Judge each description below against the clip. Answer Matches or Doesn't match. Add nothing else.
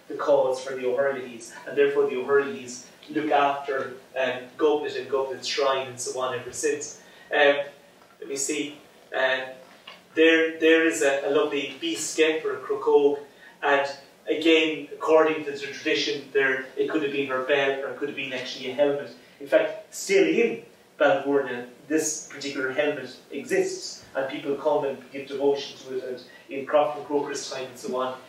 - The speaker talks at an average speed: Matches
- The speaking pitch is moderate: Matches